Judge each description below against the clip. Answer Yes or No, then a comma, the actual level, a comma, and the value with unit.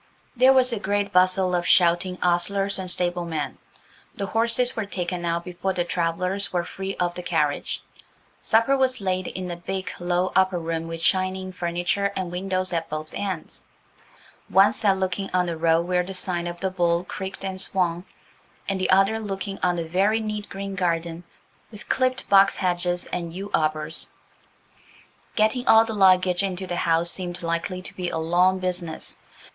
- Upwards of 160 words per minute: Yes, average, 175 wpm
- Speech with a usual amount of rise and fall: No, narrow, 2.0 semitones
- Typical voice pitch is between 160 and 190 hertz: Yes, medium, 185 Hz